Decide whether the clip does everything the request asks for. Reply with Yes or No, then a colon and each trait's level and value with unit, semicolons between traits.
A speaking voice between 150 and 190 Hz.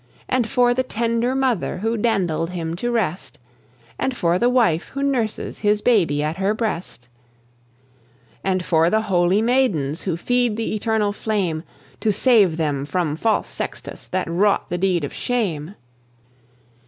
No: high, 205 Hz